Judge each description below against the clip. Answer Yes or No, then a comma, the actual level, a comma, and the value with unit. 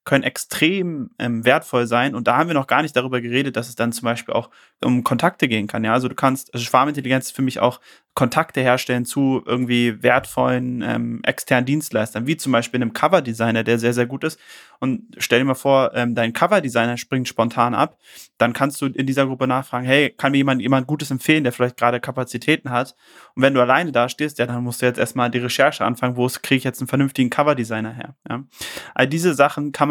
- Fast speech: Yes, fast, 225 wpm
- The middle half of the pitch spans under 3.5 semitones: Yes, narrow, 2.4 semitones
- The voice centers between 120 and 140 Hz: Yes, low, 125 Hz